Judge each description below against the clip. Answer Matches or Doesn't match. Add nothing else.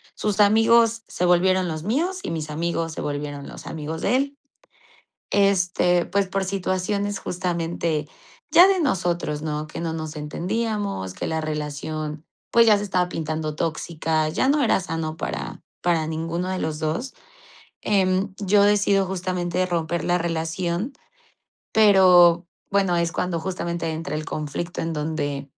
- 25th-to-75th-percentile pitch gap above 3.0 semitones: Matches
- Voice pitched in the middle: Matches